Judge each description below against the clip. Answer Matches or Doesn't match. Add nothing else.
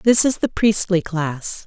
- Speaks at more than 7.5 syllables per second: Doesn't match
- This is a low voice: Doesn't match